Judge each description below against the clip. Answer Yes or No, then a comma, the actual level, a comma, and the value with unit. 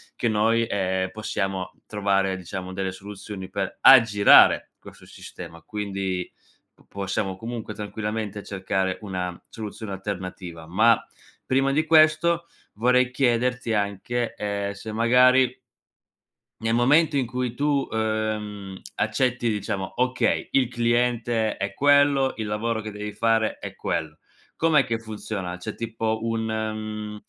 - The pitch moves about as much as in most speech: Yes, average, 3.5 semitones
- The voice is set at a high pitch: No, low, 110 Hz